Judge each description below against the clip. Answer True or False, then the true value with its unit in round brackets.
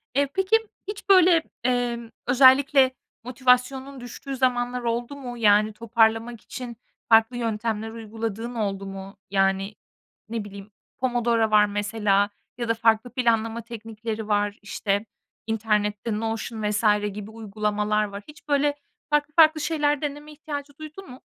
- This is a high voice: True (230 Hz)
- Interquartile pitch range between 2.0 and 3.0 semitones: False (3.7 semitones)